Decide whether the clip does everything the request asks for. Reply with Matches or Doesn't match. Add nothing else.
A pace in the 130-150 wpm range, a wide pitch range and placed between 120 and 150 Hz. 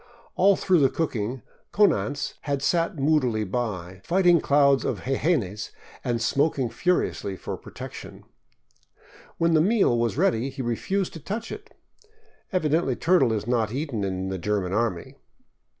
Matches